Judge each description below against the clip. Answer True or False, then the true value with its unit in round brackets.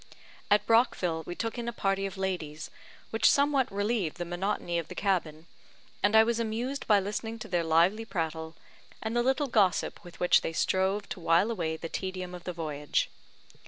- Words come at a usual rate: True (190 wpm)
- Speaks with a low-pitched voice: False (190 Hz)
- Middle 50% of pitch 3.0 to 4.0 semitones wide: False (4.8 semitones)